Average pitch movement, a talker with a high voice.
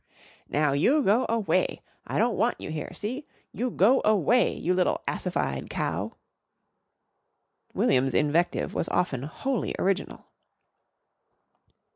No: wide, 7.8 semitones; high, 200 Hz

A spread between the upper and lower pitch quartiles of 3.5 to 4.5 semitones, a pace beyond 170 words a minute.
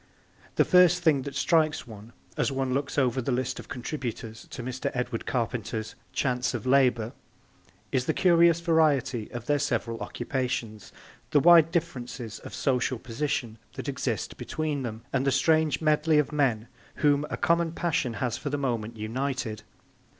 No: average, 4.1 semitones; average, 160 wpm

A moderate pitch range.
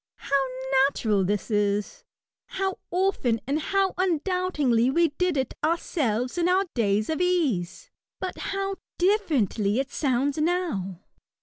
No: wide, 8.1 semitones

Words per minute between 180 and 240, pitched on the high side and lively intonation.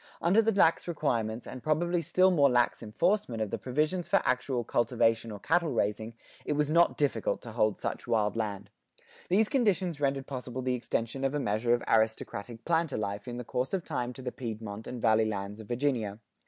No: average, 195 wpm; low, 125 Hz; wide, 5.7 semitones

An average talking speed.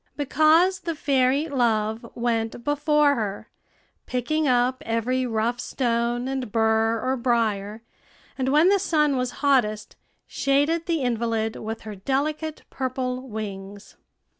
No: slow, 125 wpm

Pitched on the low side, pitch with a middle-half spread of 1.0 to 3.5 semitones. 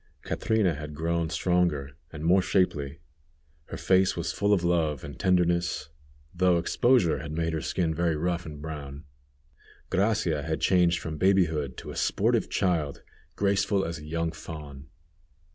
Yes: very low, 85 Hz; average, 3.0 semitones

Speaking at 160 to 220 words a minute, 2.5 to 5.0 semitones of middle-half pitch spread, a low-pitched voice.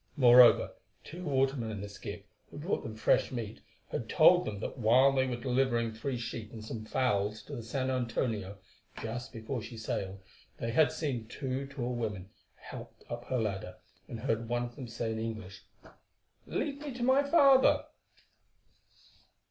Yes: average, 170 wpm; average, 3.3 semitones; low, 120 Hz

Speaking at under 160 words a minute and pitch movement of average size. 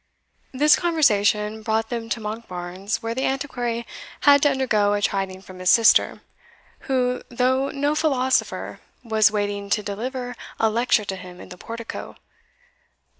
Yes: average, 145 wpm; average, 4.1 semitones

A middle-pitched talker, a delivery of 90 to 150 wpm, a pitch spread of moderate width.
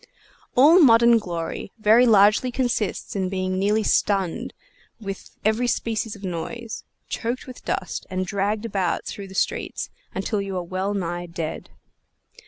No: high, 205 Hz; average, 145 wpm; average, 3.5 semitones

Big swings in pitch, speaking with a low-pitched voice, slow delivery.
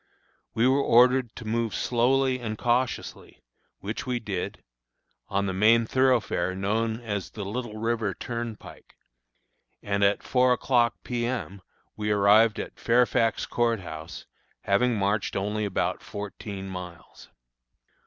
No: average, 3.1 semitones; low, 110 Hz; slow, 130 wpm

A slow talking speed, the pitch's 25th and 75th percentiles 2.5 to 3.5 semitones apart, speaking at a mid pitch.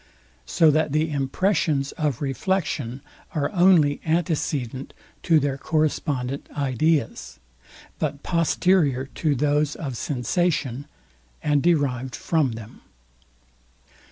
Yes: slow, 100 wpm; average, 3.1 semitones; medium, 145 Hz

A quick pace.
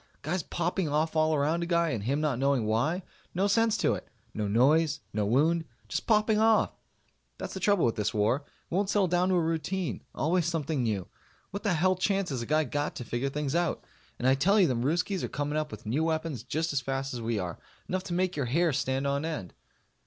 Yes: fast, 230 wpm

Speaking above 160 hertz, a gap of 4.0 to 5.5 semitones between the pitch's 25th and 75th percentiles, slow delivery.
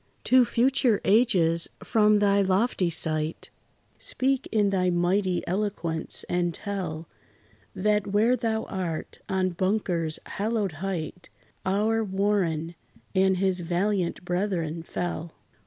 No: high, 190 Hz; average, 3.4 semitones; slow, 110 wpm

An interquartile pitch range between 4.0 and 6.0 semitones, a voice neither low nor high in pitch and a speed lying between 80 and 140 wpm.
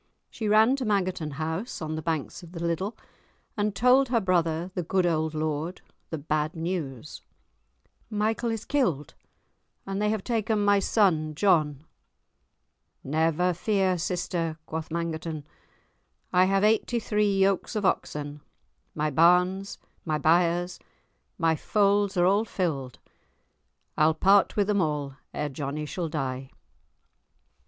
Yes: average, 4.4 semitones; medium, 175 Hz; slow, 135 wpm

